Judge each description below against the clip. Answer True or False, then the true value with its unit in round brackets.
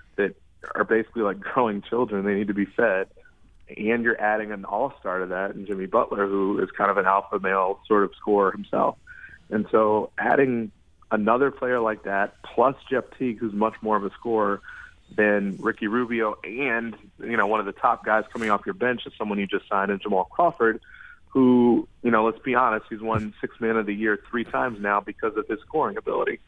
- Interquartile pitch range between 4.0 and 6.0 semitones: False (2.7 semitones)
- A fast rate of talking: True (210 wpm)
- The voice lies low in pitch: True (110 Hz)